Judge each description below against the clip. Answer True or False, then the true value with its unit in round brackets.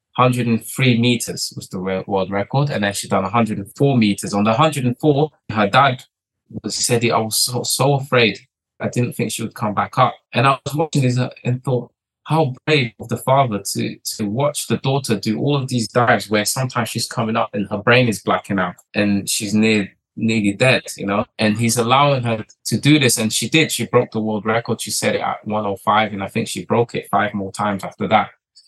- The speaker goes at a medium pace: False (220 wpm)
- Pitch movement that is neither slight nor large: True (3.6 semitones)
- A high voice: False (115 Hz)